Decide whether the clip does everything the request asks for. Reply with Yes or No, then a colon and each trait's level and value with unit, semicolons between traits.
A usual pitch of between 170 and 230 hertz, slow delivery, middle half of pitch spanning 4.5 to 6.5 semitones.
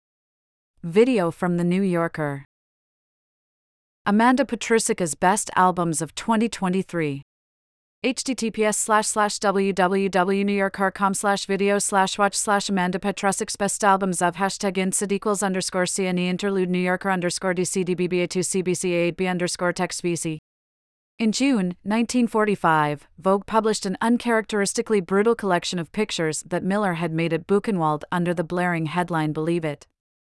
No: high, 190 Hz; slow, 120 wpm; average, 2.7 semitones